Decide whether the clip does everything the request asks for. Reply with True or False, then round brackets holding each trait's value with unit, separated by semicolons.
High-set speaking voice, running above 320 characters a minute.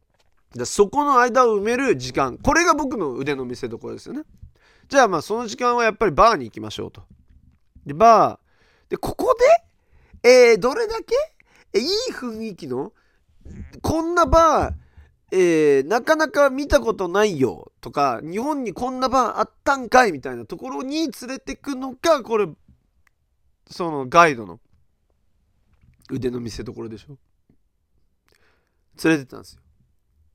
False (215 Hz; 290 characters per minute)